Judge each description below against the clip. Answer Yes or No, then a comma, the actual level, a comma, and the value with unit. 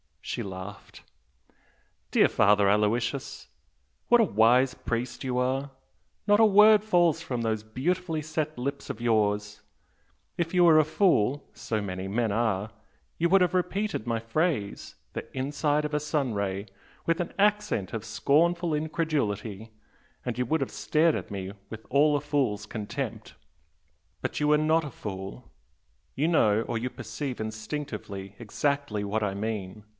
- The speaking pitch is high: No, low, 125 Hz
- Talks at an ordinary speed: Yes, average, 155 wpm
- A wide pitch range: Yes, wide, 6.7 semitones